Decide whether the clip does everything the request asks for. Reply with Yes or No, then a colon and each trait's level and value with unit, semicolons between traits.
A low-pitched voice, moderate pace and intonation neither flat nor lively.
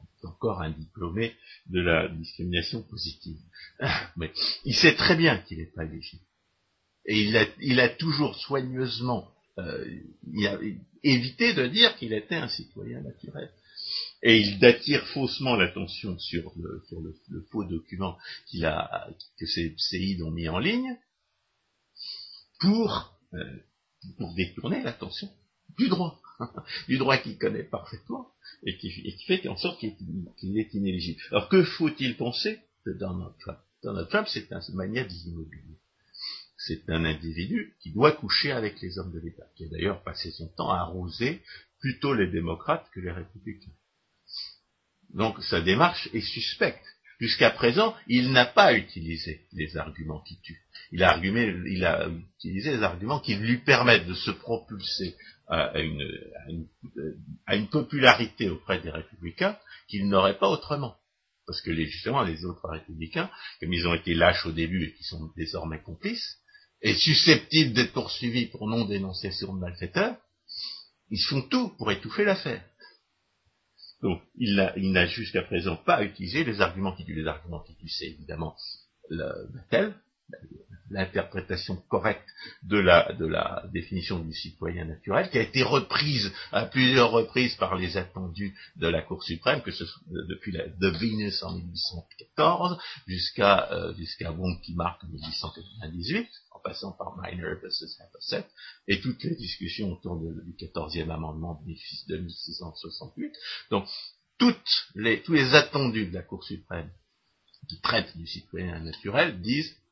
No: very low, 95 Hz; average, 155 wpm; wide, 6.6 semitones